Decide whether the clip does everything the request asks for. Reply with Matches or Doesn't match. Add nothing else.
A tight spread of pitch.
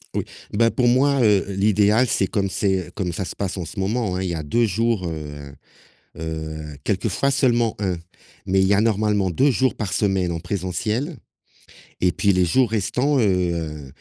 Doesn't match